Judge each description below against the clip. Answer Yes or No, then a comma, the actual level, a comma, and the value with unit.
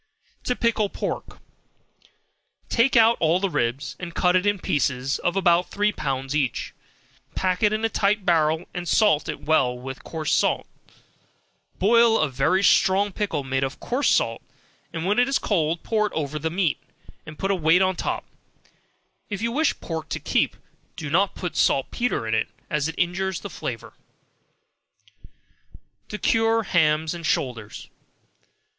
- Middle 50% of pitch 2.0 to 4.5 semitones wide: No, average, 5.2 semitones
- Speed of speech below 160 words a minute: No, average, 165 wpm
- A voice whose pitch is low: No, medium, 175 Hz